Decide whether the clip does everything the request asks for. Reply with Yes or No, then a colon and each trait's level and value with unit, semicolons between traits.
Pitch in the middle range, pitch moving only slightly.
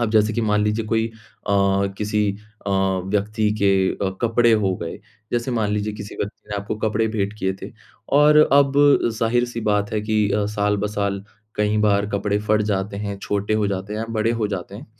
No: low, 105 Hz; narrow, 1.6 semitones